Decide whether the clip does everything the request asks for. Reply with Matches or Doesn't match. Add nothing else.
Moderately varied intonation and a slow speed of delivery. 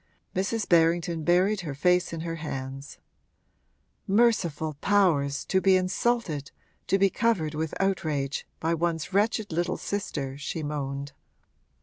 Matches